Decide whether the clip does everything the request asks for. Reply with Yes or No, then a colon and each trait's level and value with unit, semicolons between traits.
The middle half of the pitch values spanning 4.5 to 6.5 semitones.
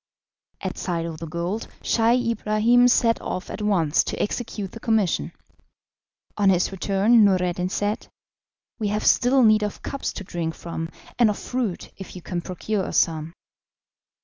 No: average, 4.1 semitones